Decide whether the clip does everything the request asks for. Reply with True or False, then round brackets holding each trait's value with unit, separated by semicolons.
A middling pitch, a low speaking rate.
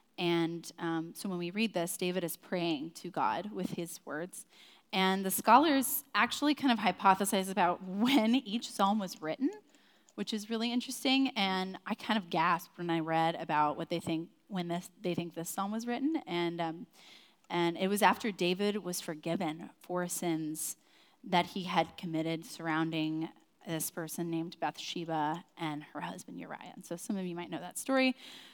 False (180 Hz; 180 wpm)